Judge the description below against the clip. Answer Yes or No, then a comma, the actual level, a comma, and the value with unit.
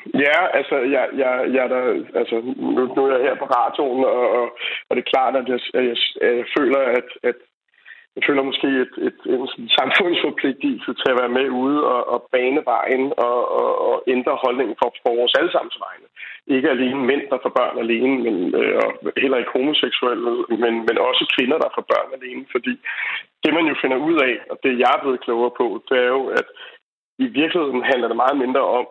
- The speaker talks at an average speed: Yes, average, 170 wpm